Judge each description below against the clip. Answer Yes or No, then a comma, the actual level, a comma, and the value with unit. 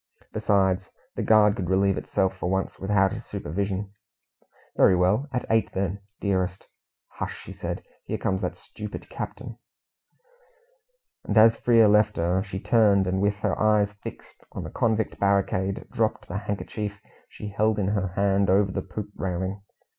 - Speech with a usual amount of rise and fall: No, narrow, 1.8 semitones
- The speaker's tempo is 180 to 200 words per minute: No, average, 160 wpm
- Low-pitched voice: Yes, low, 100 Hz